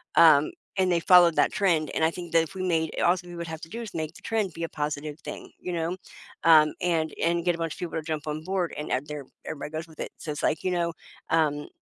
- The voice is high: No, medium, 165 Hz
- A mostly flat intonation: Yes, narrow, 2.2 semitones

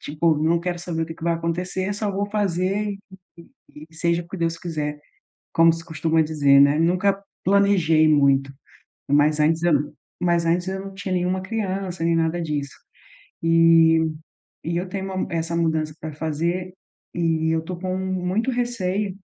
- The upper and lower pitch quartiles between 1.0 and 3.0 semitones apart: Yes, narrow, 2.6 semitones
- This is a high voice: No, medium, 170 Hz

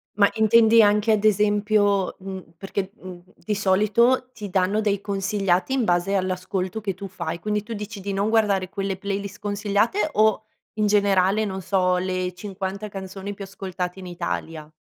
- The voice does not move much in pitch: Yes, narrow, 1.9 semitones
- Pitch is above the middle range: Yes, high, 200 Hz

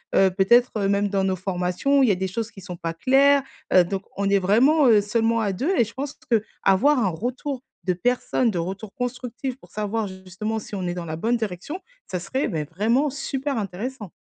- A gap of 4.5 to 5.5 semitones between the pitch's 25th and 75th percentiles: Yes, average, 5.0 semitones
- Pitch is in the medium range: No, high, 210 Hz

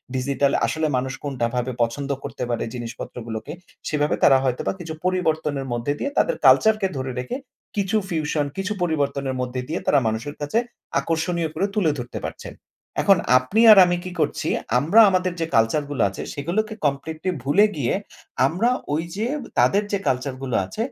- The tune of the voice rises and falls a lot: Yes, wide, 5.7 semitones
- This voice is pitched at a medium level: Yes, medium, 145 Hz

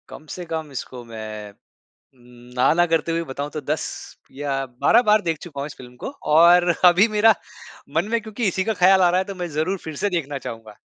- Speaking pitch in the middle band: Yes, medium, 160 Hz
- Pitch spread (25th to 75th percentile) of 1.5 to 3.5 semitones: No, average, 4.9 semitones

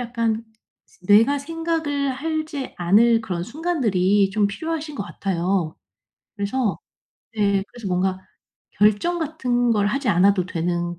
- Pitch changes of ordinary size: No, wide, 6.5 semitones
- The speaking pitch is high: Yes, high, 220 Hz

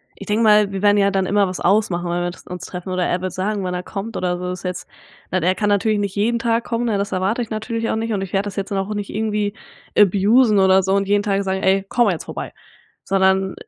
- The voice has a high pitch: Yes, high, 200 Hz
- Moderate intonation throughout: No, narrow, 2.1 semitones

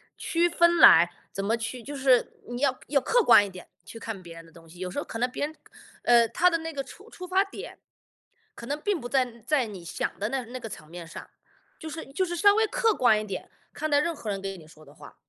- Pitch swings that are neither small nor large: No, wide, 8.1 semitones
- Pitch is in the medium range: No, very high, 250 Hz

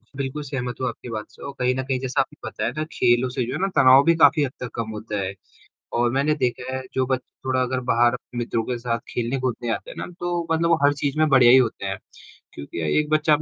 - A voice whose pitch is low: Yes, low, 130 Hz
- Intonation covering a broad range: No, narrow, 2.6 semitones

